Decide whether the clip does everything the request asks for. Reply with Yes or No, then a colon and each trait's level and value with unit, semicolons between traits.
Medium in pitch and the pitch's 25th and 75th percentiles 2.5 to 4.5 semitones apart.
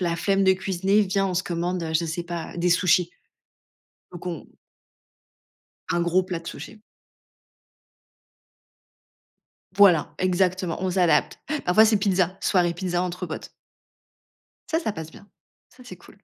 No: medium, 180 Hz; narrow, 1.9 semitones